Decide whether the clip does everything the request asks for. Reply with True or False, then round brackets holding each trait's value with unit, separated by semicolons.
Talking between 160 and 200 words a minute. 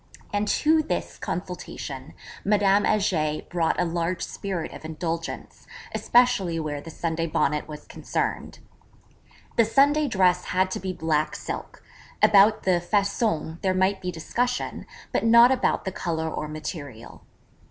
False (140 wpm)